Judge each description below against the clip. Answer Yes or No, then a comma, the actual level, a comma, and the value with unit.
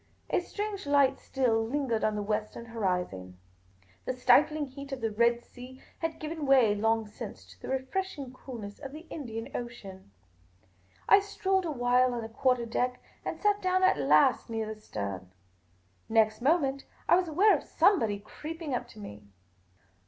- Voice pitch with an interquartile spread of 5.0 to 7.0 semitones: Yes, wide, 5.4 semitones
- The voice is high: Yes, very high, 250 Hz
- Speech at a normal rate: Yes, average, 165 wpm